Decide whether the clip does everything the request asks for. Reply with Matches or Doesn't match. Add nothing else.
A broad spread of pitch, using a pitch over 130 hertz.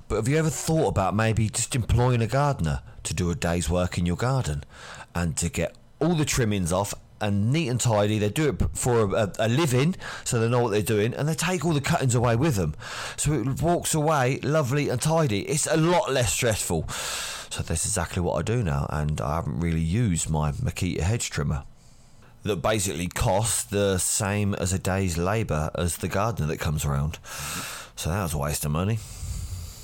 Doesn't match